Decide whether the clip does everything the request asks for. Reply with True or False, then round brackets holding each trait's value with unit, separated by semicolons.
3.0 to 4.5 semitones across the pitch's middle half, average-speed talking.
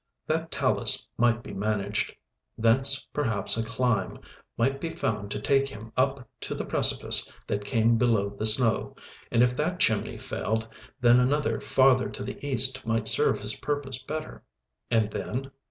True (3.5 semitones; 160 wpm)